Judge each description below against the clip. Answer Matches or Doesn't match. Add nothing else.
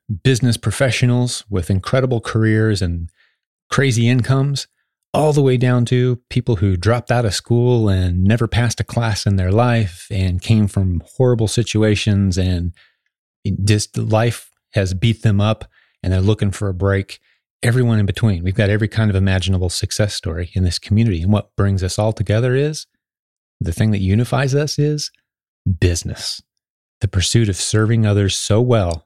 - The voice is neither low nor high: Doesn't match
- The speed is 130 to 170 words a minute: Matches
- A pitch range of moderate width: Matches